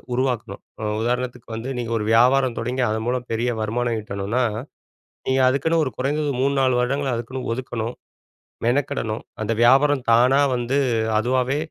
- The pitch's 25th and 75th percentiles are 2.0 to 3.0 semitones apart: Yes, narrow, 2.4 semitones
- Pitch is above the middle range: No, low, 125 Hz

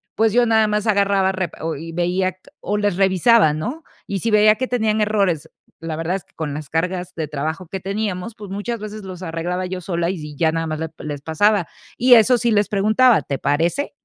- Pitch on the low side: No, high, 190 Hz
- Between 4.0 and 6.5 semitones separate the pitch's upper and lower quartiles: Yes, average, 4.4 semitones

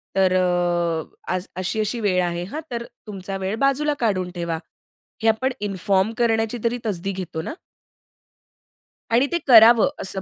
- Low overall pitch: No, high, 205 Hz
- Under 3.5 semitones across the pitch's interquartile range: No, average, 3.9 semitones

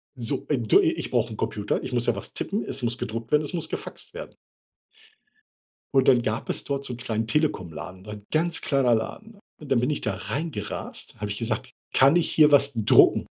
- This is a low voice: Yes, low, 125 Hz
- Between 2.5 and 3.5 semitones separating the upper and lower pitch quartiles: No, average, 5.1 semitones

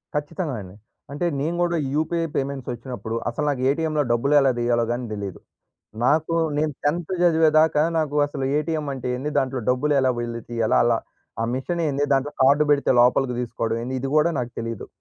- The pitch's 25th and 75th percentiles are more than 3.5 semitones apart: Yes, average, 3.9 semitones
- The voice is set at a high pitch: No, medium, 140 Hz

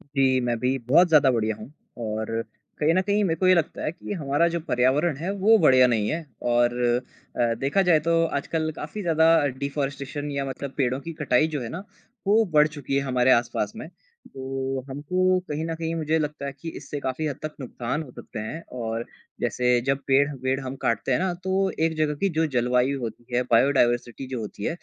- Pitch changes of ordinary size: Yes, average, 4.4 semitones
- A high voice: No, medium, 140 Hz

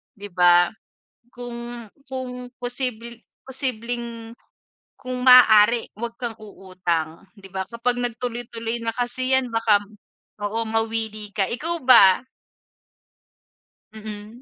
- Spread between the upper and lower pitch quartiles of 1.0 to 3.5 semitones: Yes, narrow, 2.6 semitones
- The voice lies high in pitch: Yes, high, 230 Hz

